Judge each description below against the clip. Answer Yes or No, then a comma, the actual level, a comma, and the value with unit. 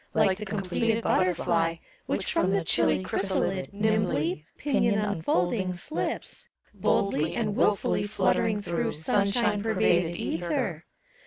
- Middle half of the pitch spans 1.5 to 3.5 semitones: Yes, average, 3.2 semitones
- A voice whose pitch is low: No, high, 195 Hz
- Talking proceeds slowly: Yes, slow, 110 wpm